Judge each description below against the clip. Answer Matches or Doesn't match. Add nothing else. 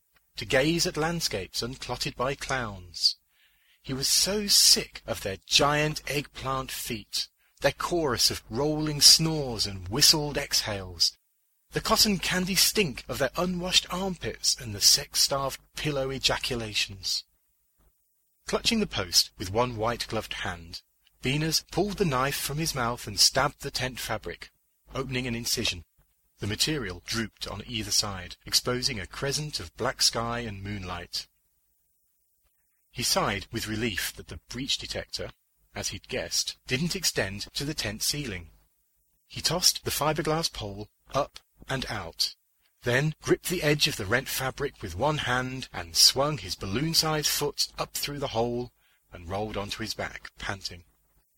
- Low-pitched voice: Matches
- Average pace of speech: Matches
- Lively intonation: Matches